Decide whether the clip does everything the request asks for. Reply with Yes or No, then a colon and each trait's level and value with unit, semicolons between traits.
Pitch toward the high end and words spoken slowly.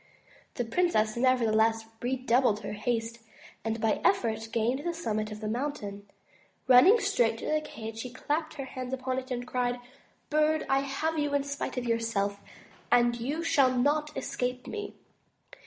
No: very high, 250 Hz; average, 160 wpm